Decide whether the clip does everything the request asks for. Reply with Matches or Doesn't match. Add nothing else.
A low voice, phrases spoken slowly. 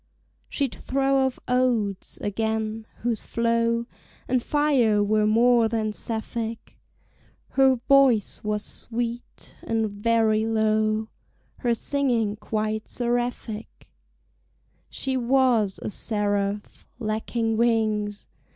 Doesn't match